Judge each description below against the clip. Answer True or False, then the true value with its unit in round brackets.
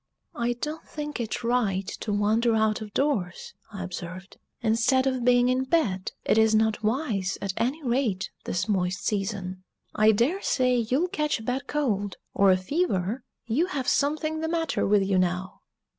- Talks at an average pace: True (170 wpm)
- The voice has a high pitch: True (225 Hz)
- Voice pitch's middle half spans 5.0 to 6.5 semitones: True (5.4 semitones)